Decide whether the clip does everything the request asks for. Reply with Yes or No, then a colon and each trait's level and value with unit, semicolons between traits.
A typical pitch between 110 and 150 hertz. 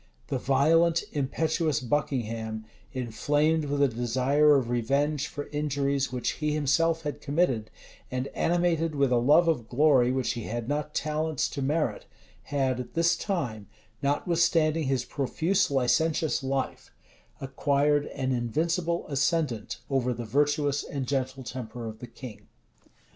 Yes: medium, 140 Hz